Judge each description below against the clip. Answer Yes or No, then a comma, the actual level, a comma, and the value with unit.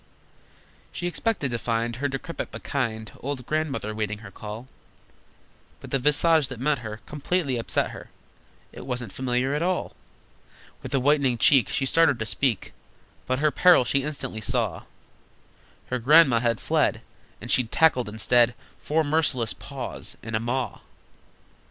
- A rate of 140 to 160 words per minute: Yes, average, 150 wpm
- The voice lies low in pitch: Yes, low, 130 Hz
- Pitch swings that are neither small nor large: Yes, average, 4.3 semitones